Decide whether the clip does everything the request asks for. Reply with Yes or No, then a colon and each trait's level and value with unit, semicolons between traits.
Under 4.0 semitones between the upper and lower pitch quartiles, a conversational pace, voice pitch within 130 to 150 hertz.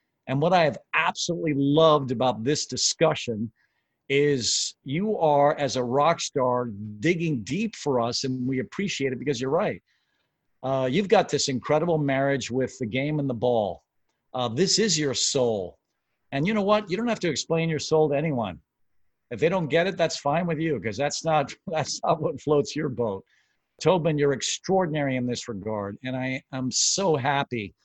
No: average, 4.4 semitones; average, 185 wpm; medium, 140 Hz